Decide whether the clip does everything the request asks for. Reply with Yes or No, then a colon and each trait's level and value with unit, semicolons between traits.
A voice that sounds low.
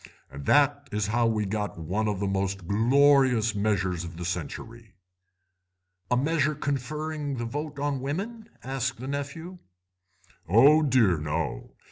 Yes: low, 120 Hz